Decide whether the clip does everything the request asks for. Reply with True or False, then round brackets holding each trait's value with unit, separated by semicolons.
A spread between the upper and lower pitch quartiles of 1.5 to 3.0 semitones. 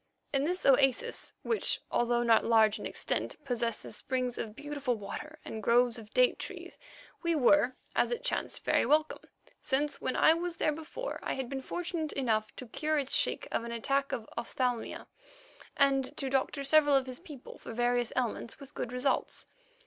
False (3.7 semitones)